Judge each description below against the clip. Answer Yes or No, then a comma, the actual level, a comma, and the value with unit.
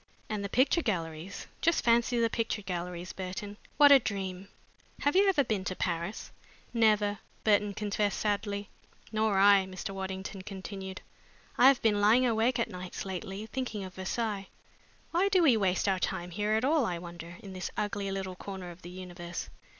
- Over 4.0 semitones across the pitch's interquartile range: No, average, 3.2 semitones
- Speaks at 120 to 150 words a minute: No, average, 175 wpm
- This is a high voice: Yes, high, 200 Hz